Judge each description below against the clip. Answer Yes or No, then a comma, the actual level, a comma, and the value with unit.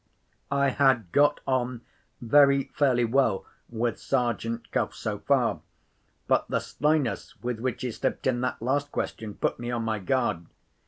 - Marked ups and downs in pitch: No, average, 2.9 semitones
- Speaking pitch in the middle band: No, low, 125 Hz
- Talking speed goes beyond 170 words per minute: No, average, 155 wpm